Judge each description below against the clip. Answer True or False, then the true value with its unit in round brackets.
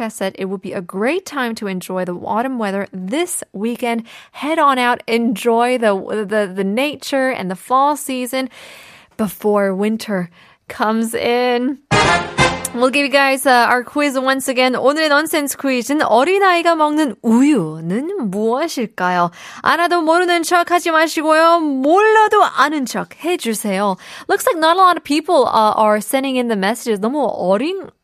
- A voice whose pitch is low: False (255 Hz)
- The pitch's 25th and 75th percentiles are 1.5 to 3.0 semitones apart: False (6.1 semitones)